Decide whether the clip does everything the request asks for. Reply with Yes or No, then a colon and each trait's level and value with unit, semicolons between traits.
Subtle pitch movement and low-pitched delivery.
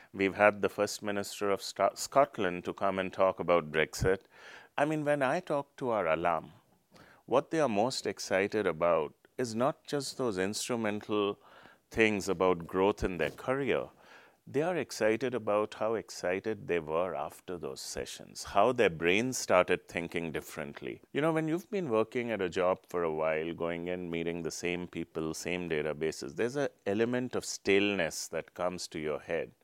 No: average, 4.3 semitones; very low, 95 Hz